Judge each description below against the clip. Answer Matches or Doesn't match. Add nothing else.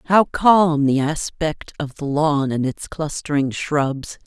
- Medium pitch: Matches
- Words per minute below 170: Matches